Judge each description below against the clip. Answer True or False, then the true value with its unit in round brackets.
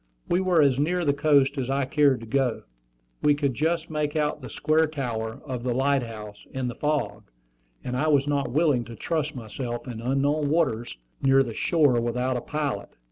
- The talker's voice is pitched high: False (140 Hz)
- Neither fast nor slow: True (195 wpm)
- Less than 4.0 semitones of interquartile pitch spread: True (3.5 semitones)